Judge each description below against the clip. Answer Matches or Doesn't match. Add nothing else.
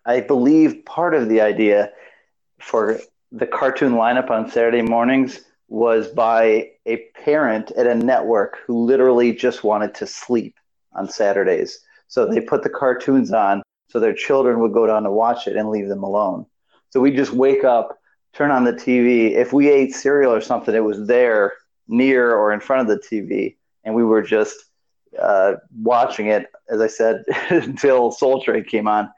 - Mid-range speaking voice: Doesn't match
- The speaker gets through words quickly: Doesn't match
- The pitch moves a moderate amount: Matches